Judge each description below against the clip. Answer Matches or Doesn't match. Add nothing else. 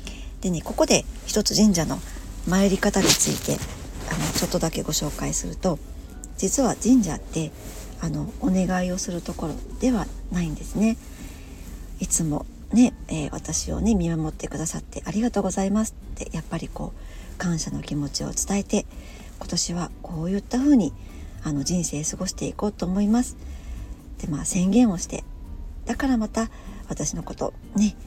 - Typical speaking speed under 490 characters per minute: Matches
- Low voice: Doesn't match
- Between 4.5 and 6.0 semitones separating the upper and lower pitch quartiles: Matches